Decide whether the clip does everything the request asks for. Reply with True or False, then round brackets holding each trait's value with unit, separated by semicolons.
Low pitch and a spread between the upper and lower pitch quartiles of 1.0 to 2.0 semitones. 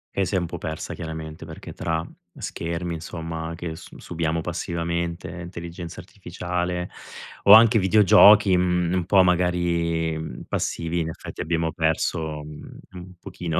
True (85 Hz; 1.7 semitones)